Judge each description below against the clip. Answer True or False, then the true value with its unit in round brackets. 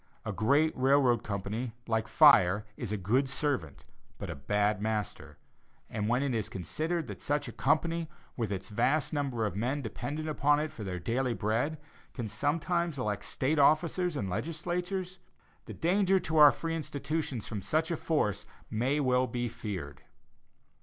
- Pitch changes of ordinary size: False (6.4 semitones)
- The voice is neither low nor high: False (130 Hz)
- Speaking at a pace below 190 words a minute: True (165 wpm)